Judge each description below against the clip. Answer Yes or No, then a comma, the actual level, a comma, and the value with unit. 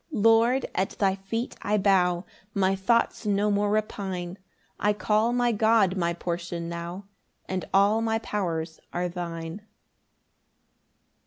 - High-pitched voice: Yes, high, 195 Hz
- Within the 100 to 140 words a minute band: Yes, slow, 135 wpm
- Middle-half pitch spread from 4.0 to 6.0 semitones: No, average, 3.4 semitones